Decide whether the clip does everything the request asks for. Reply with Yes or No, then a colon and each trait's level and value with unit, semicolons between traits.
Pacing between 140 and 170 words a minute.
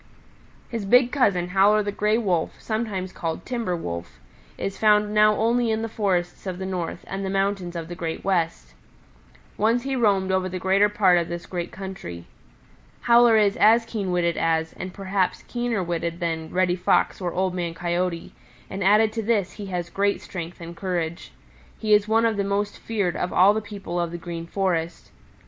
No: average, 190 wpm